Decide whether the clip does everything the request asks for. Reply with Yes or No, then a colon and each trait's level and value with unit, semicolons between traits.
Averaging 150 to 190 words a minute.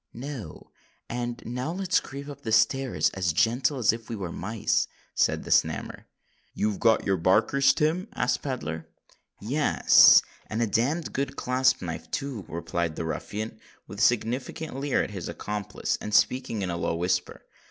Yes: average, 160 wpm